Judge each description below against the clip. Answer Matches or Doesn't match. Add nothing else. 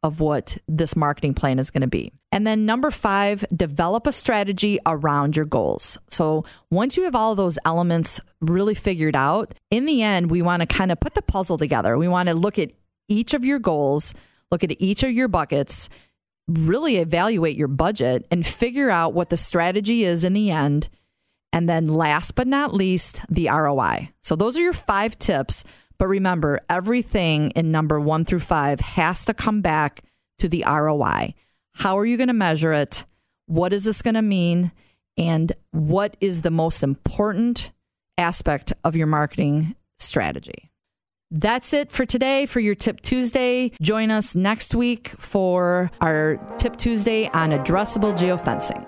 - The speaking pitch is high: Doesn't match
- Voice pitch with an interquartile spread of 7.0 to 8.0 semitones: Doesn't match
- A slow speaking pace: Doesn't match